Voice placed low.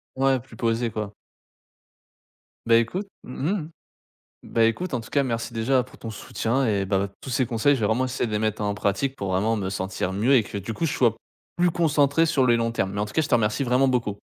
Yes: low, 115 Hz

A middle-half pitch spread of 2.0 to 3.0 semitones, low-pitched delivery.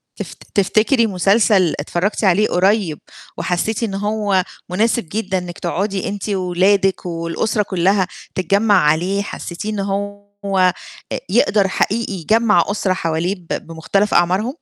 No: narrow, 2.6 semitones; high, 195 Hz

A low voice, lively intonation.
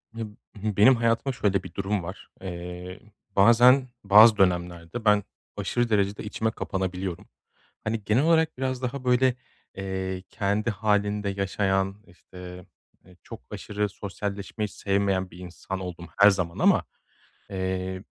No: low, 100 Hz; average, 2.8 semitones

